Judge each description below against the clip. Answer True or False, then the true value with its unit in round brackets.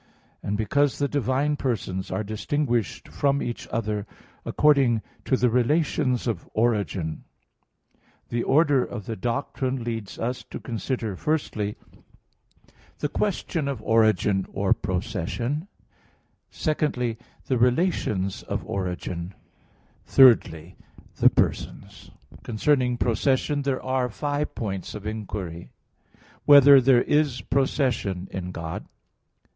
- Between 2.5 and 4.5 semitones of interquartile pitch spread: False (5.2 semitones)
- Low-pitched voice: True (120 Hz)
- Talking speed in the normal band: False (110 wpm)